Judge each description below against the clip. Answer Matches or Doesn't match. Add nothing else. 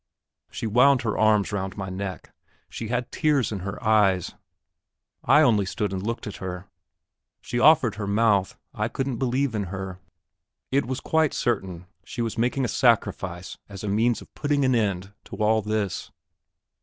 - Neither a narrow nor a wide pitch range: Matches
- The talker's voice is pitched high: Doesn't match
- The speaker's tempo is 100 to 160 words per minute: Doesn't match